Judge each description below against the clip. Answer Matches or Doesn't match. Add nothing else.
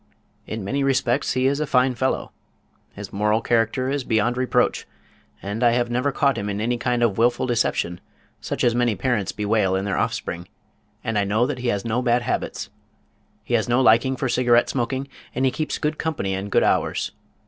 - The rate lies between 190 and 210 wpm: Matches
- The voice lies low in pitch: Matches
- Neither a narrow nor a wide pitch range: Matches